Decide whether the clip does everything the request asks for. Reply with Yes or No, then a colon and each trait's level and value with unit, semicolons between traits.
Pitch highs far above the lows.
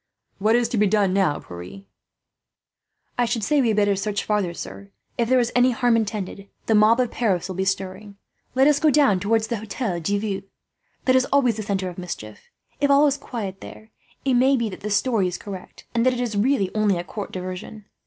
No: average, 4.1 semitones